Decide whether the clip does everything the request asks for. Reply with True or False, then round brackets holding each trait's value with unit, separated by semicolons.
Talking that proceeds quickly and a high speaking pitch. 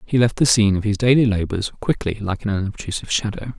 False (220 wpm; 105 Hz)